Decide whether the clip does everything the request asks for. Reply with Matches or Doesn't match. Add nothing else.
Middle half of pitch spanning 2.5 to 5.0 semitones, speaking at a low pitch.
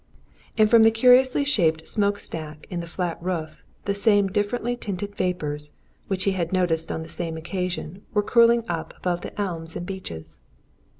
Doesn't match